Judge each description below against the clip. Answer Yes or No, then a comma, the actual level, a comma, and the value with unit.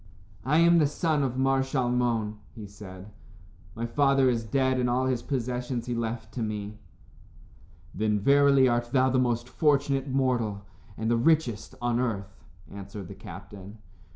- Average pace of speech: Yes, average, 155 wpm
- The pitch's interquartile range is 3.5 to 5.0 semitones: Yes, average, 3.8 semitones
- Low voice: Yes, low, 120 Hz